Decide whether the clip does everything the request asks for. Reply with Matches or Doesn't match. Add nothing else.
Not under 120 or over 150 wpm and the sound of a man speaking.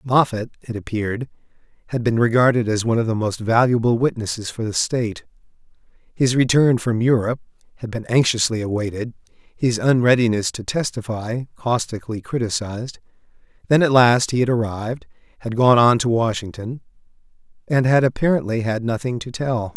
Matches